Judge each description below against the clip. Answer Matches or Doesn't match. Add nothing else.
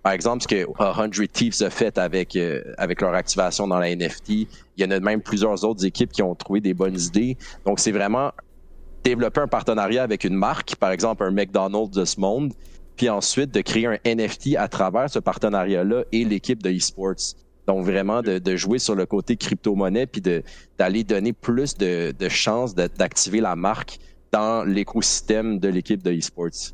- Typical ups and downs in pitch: Matches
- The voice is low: Matches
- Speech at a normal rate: Matches